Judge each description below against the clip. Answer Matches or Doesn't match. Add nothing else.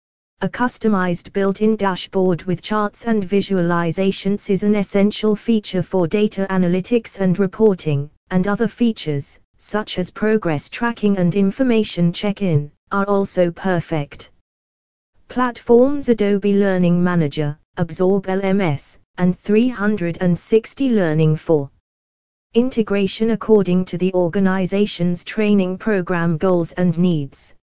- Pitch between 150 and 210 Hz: Matches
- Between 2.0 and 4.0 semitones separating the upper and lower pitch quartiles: Matches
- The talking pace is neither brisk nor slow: Doesn't match